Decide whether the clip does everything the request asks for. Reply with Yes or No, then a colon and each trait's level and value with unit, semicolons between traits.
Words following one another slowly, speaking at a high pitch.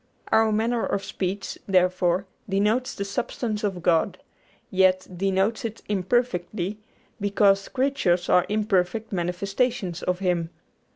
Yes: slow, 115 wpm; high, 195 Hz